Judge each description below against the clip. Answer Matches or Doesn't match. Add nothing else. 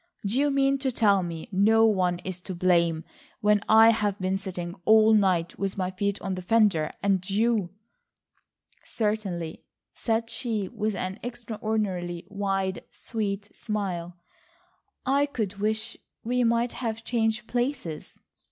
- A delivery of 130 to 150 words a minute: Matches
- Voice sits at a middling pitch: Doesn't match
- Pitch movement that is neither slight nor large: Matches